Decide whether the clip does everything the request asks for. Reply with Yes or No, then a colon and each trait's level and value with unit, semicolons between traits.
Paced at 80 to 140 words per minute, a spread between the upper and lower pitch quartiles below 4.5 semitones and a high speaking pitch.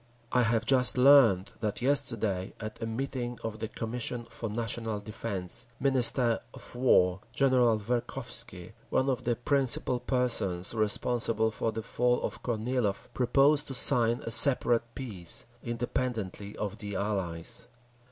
No: slow, 135 wpm; average, 2.7 semitones; low, 115 Hz